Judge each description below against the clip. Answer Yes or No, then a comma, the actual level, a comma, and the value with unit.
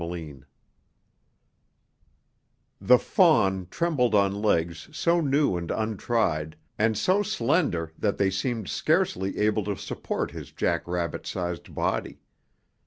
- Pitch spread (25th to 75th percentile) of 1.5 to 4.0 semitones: No, average, 5.3 semitones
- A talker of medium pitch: No, low, 100 Hz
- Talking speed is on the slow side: Yes, slow, 120 wpm